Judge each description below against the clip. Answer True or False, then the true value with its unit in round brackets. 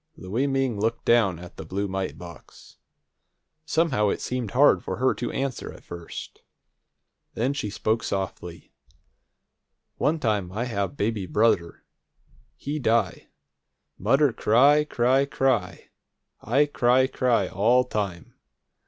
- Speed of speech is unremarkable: False (125 wpm)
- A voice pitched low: True (115 Hz)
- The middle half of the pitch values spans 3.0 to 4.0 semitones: False (5.1 semitones)